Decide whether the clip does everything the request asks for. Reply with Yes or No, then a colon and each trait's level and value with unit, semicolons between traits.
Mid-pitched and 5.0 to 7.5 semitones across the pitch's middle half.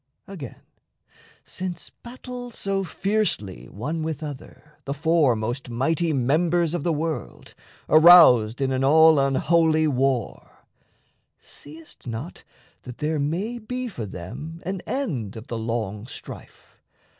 Yes: medium, 155 Hz; wide, 5.4 semitones